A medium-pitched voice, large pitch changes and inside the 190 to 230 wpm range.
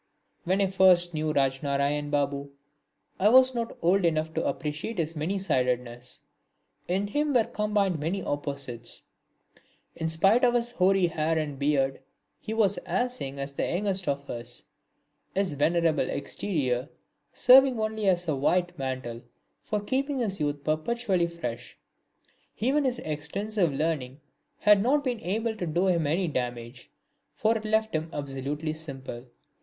No: medium, 170 Hz; wide, 6.7 semitones; average, 150 wpm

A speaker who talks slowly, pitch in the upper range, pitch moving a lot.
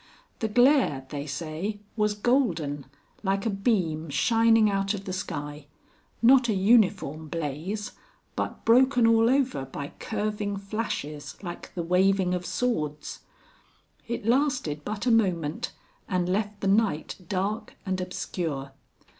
Yes: slow, 130 wpm; high, 195 Hz; wide, 6.0 semitones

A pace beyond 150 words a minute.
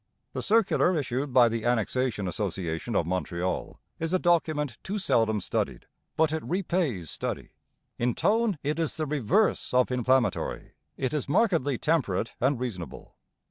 No: average, 145 wpm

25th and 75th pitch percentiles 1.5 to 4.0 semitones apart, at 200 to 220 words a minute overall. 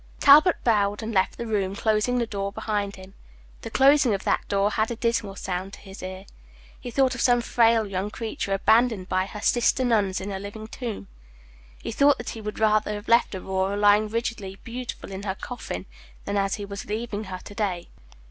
Yes: average, 2.9 semitones; fast, 205 wpm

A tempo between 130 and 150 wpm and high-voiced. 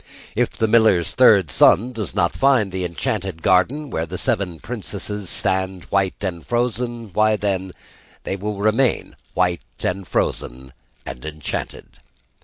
No: average, 140 wpm; low, 100 Hz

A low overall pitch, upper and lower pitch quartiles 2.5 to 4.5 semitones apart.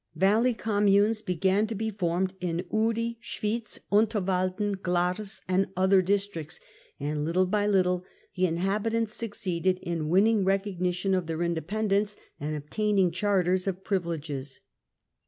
No: high, 190 Hz; average, 2.9 semitones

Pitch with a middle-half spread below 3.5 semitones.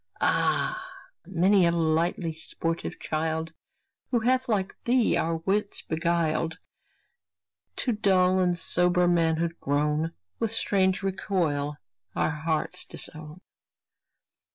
Yes: average, 3.1 semitones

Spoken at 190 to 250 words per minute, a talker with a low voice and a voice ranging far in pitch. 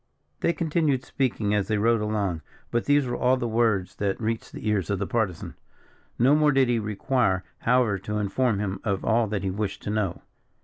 No: fast, 205 wpm; low, 110 Hz; average, 3.7 semitones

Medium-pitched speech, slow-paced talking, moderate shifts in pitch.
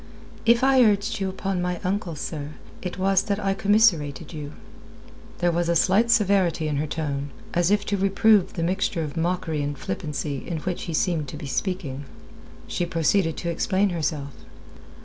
No: medium, 175 Hz; average, 175 wpm; average, 4.1 semitones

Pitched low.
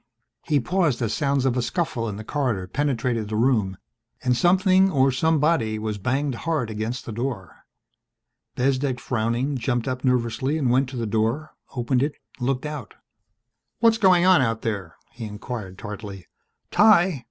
Yes: low, 125 Hz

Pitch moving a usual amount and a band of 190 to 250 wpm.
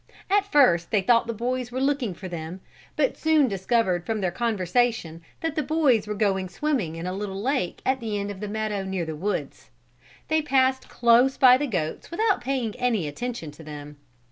No: wide, 5.9 semitones; average, 195 wpm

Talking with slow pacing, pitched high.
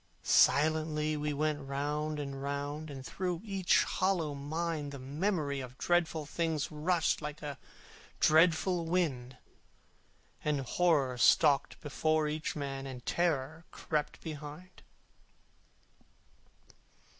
No: slow, 110 wpm; medium, 150 Hz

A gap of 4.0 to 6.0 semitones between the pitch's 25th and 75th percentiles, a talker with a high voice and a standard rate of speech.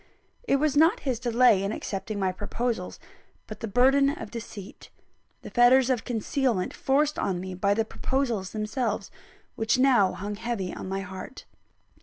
Yes: average, 4.8 semitones; high, 225 Hz; average, 160 wpm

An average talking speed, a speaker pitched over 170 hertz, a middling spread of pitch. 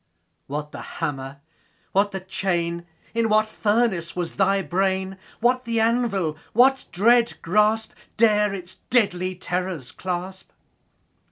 No: slow, 125 wpm; high, 190 Hz; average, 3.9 semitones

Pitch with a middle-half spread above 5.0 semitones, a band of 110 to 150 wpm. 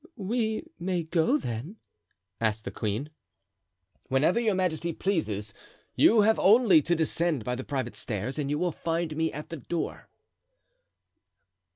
Yes: wide, 5.5 semitones; average, 145 wpm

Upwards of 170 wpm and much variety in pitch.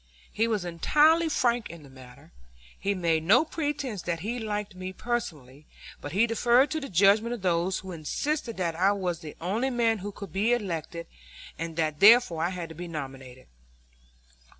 Yes: average, 180 wpm; wide, 6.0 semitones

